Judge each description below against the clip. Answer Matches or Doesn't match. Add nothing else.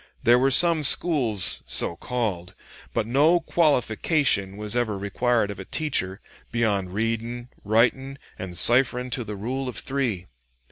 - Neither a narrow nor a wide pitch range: Matches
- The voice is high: Doesn't match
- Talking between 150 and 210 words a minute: Doesn't match